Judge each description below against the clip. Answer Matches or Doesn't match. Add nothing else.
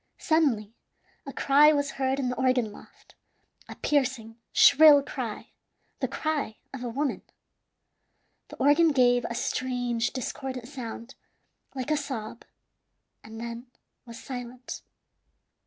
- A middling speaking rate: Doesn't match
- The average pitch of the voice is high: Matches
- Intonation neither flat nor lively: Matches